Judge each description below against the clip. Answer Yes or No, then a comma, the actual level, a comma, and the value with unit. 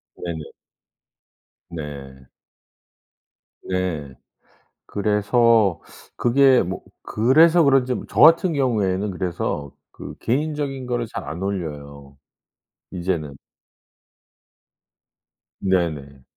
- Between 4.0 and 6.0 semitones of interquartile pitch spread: No, wide, 8.2 semitones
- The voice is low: Yes, very low, 95 Hz